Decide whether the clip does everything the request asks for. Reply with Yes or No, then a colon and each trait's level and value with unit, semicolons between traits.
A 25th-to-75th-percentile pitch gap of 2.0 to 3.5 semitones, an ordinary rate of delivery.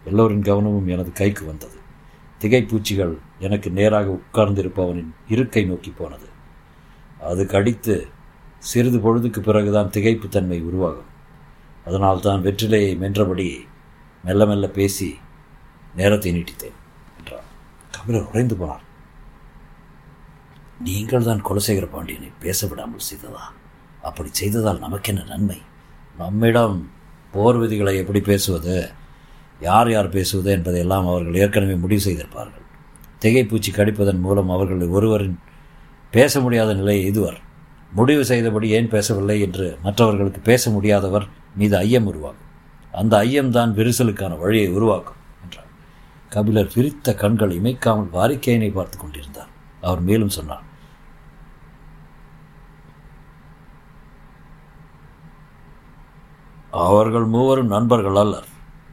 Yes: average, 3.2 semitones; average, 100 wpm